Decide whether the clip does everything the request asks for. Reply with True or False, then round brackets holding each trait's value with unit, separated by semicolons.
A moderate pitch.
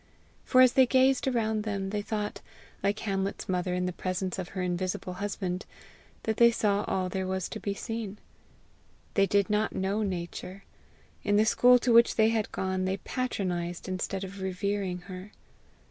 False (195 Hz)